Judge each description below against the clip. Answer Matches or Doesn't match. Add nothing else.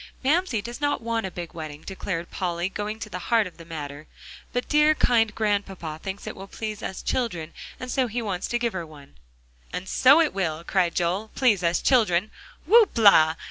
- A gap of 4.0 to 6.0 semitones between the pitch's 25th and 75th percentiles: Matches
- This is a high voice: Matches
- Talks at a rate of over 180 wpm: Matches